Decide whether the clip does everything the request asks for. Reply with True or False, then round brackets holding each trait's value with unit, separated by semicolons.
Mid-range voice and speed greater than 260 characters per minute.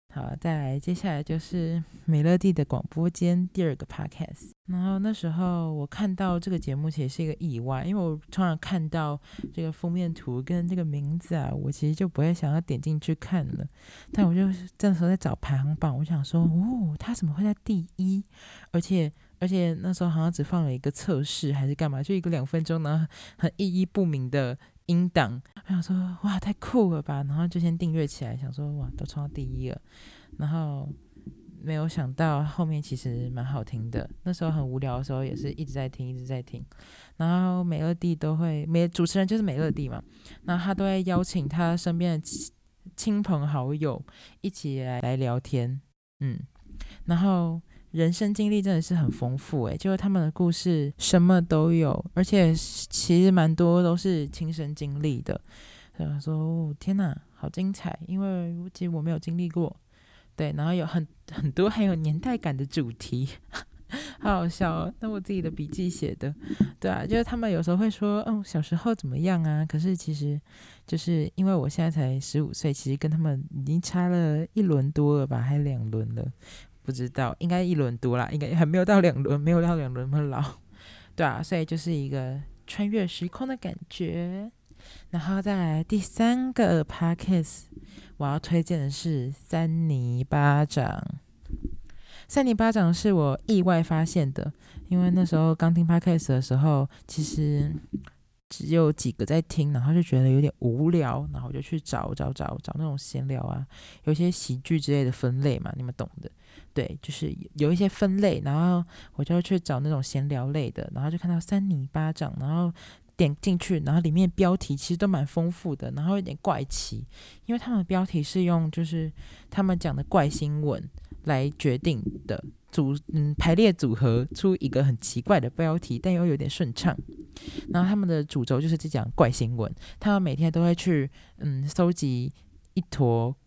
True (160 Hz; 280 characters per minute)